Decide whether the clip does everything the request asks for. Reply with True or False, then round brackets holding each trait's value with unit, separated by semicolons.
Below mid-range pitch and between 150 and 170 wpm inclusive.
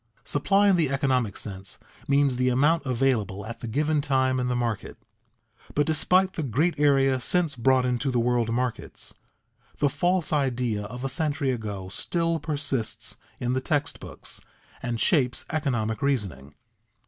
True (130 Hz; 155 wpm)